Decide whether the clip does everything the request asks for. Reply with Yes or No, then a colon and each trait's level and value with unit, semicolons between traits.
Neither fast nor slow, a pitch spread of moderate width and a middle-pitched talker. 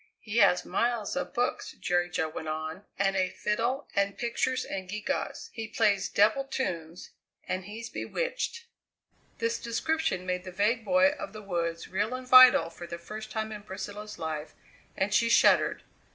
No: average, 165 wpm; average, 4.5 semitones; high, 210 Hz